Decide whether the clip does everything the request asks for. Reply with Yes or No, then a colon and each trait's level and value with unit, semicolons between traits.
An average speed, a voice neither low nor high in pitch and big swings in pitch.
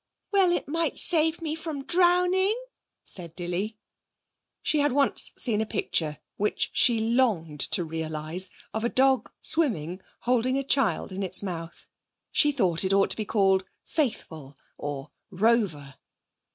No: average, 145 wpm; high, 220 Hz; wide, 8.6 semitones